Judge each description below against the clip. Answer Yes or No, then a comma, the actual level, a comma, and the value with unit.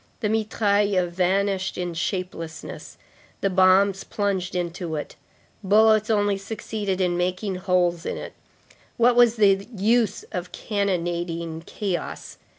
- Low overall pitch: No, high, 190 Hz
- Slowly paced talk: Yes, slow, 120 wpm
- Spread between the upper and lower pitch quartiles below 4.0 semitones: Yes, narrow, 2.5 semitones